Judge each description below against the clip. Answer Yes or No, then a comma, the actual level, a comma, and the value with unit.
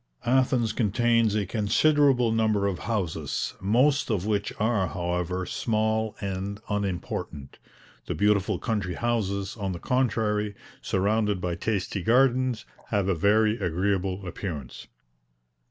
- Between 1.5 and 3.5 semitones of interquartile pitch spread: Yes, average, 3.1 semitones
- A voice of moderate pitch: No, low, 105 Hz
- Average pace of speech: No, slow, 120 wpm